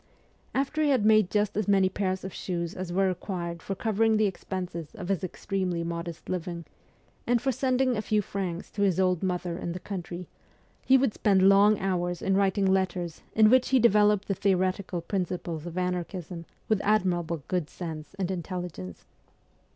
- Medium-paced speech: Yes, average, 175 wpm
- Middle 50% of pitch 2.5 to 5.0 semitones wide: Yes, average, 2.9 semitones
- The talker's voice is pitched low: No, high, 190 Hz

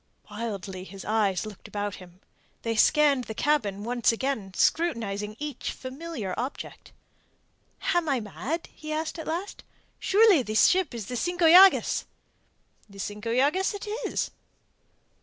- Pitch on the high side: Yes, high, 245 Hz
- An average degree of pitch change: No, wide, 7.4 semitones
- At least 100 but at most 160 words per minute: Yes, average, 140 wpm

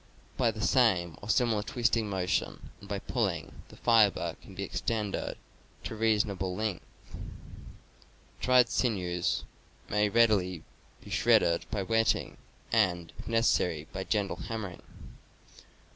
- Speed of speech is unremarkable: No, slow, 130 wpm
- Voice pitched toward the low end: Yes, low, 105 Hz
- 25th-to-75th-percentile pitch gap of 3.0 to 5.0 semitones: Yes, average, 3.6 semitones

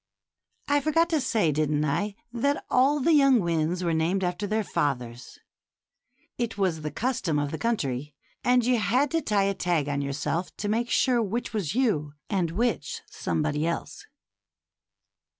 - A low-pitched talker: No, high, 195 Hz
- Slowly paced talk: No, average, 165 wpm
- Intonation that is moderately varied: No, wide, 7.8 semitones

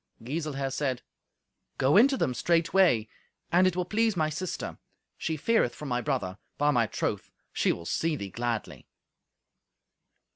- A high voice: No, medium, 150 Hz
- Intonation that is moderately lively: No, wide, 6.3 semitones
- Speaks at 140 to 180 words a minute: Yes, average, 150 wpm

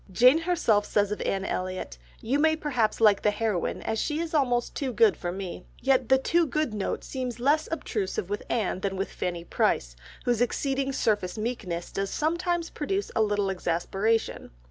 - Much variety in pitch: Yes, wide, 6.6 semitones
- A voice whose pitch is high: Yes, high, 225 Hz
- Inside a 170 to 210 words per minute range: Yes, average, 180 wpm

